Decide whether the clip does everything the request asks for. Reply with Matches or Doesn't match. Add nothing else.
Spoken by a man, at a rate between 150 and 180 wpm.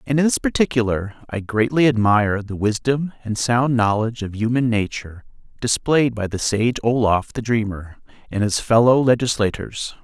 Matches